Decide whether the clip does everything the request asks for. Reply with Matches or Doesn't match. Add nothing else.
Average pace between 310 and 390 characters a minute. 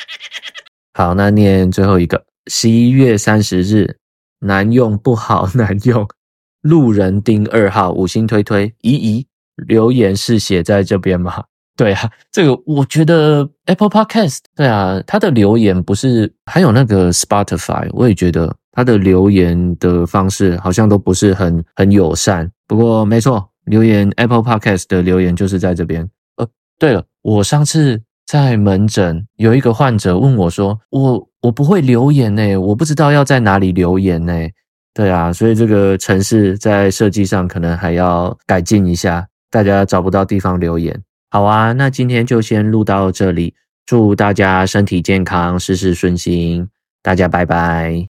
Doesn't match